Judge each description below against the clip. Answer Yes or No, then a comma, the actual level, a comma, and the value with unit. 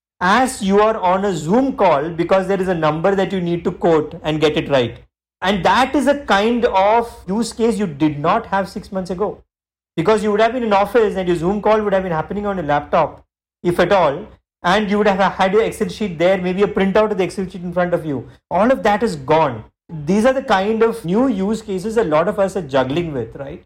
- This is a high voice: Yes, high, 195 Hz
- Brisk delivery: Yes, fast, 250 wpm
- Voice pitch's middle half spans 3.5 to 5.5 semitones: Yes, average, 3.9 semitones